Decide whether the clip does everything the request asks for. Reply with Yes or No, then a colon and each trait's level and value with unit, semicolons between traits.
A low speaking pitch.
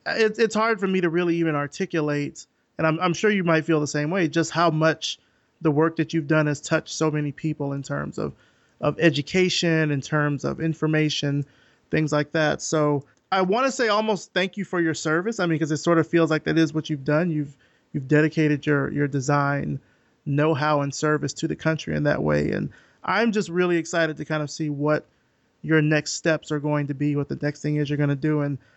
No: medium, 155 Hz